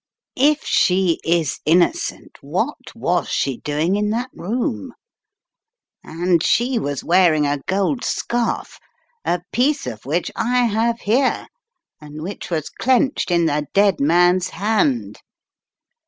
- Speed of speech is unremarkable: No, slow, 125 wpm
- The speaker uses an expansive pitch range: Yes, wide, 6.6 semitones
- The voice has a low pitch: No, medium, 185 Hz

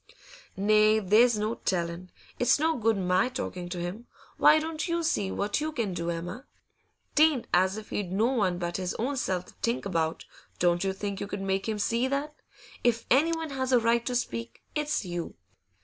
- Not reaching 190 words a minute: No, average, 195 wpm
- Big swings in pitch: Yes, wide, 5.9 semitones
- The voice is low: No, high, 215 Hz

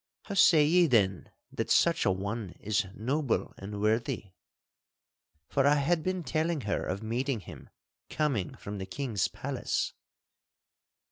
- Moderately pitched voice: No, low, 120 Hz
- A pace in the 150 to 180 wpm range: No, average, 140 wpm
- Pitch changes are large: Yes, wide, 6.8 semitones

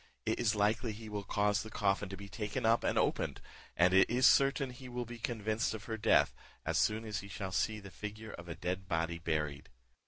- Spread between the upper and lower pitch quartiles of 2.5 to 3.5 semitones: Yes, average, 2.8 semitones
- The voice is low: Yes, low, 105 Hz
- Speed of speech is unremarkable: No, fast, 225 wpm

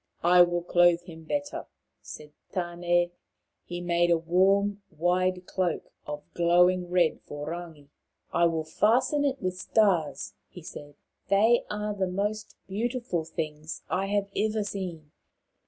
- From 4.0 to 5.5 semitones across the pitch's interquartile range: No, average, 3.0 semitones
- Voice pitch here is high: No, medium, 175 Hz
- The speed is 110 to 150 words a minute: Yes, average, 145 wpm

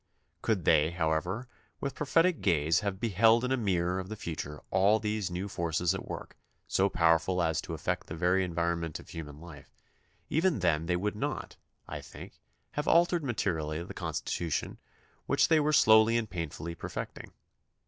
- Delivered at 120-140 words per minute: No, average, 170 wpm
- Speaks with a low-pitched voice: Yes, very low, 90 Hz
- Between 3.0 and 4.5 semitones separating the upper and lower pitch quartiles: No, average, 4.9 semitones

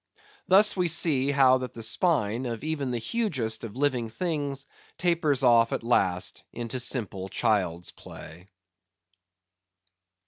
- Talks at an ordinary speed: No, slow, 130 wpm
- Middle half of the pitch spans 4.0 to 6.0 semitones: Yes, average, 5.0 semitones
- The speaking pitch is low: Yes, low, 130 Hz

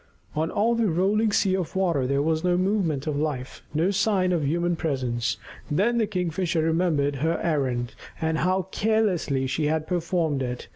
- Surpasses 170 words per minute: Yes, average, 180 wpm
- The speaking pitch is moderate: Yes, medium, 165 Hz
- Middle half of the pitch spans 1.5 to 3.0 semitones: No, average, 4.5 semitones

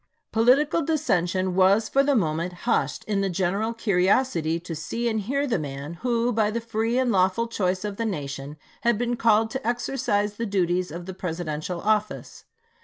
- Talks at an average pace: Yes, average, 180 wpm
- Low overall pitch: No, high, 205 Hz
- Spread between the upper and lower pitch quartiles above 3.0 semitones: Yes, average, 4.7 semitones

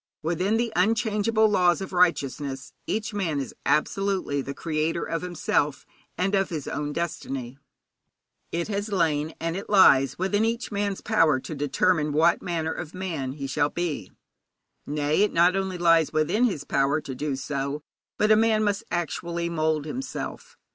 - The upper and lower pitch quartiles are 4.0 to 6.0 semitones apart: Yes, average, 5.0 semitones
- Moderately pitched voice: Yes, medium, 170 Hz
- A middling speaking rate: Yes, average, 160 wpm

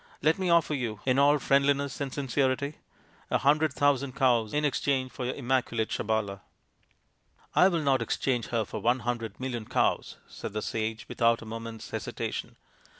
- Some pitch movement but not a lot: Yes, average, 3.6 semitones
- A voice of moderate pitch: No, low, 130 Hz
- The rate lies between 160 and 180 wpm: Yes, average, 170 wpm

